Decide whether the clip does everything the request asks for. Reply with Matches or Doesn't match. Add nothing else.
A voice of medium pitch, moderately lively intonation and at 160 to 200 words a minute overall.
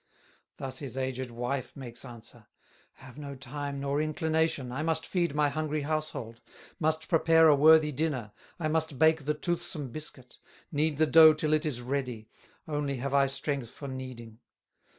Matches